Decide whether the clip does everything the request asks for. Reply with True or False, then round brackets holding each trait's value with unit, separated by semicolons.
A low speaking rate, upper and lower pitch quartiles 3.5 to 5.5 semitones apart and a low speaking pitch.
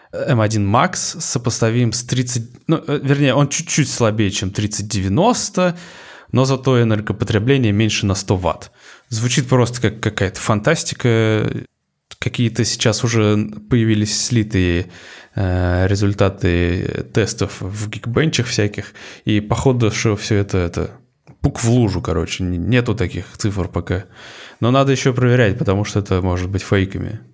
False (130 wpm; 4.1 semitones; 110 Hz)